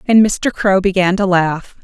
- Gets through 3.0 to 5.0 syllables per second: Yes, 4.2 syllables/s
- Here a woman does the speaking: Yes, female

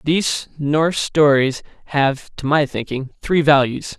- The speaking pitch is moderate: Yes, medium, 145 Hz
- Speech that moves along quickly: No, slow, 135 wpm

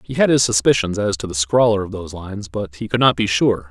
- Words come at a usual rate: No, fast, 275 wpm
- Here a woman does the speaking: No, male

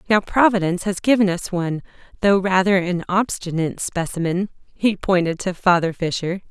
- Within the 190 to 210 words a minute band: No, average, 150 wpm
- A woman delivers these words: Yes, female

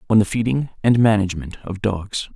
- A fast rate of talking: No, average, 180 wpm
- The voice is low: Yes, low, 105 Hz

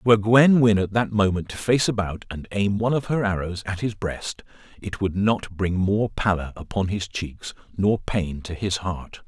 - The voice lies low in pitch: Yes, low, 100 Hz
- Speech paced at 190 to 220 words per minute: Yes, fast, 205 wpm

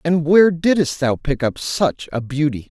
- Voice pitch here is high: No, medium, 150 Hz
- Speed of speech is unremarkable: Yes, average, 195 wpm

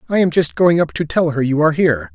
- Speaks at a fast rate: Yes, fast, 310 wpm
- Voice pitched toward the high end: No, medium, 150 Hz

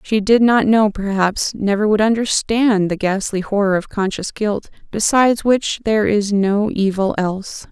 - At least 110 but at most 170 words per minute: Yes, average, 165 wpm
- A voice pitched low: No, high, 205 Hz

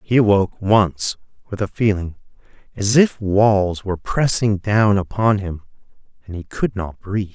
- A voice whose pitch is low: Yes, low, 100 Hz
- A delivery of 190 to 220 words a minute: No, average, 155 wpm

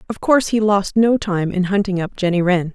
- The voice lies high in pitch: Yes, high, 195 Hz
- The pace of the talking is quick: Yes, fast, 240 wpm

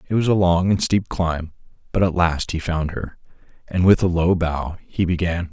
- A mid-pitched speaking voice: No, very low, 90 Hz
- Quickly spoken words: Yes, fast, 215 wpm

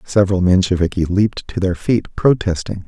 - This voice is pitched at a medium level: No, very low, 95 Hz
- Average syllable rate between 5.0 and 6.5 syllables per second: Yes, 5.4 syllables/s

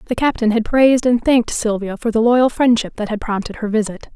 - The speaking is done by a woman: Yes, female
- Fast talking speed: Yes, fast, 230 wpm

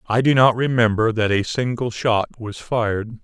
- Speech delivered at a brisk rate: No, average, 185 wpm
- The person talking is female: No, male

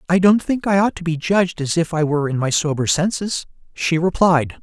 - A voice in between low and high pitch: Yes, medium, 170 Hz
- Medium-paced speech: No, fast, 235 wpm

